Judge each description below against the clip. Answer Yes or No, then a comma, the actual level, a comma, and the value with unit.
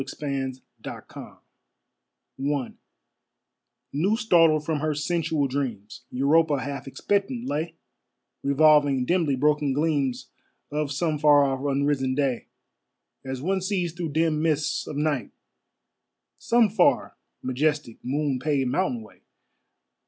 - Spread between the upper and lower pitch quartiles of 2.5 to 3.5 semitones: Yes, average, 3.0 semitones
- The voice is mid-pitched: Yes, medium, 145 Hz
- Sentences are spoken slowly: Yes, slow, 115 wpm